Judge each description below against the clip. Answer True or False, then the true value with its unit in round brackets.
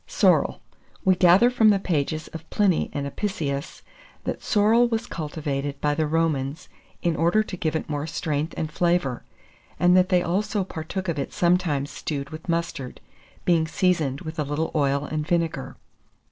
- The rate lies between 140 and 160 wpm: False (175 wpm)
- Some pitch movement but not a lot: True (3.6 semitones)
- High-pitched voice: False (160 Hz)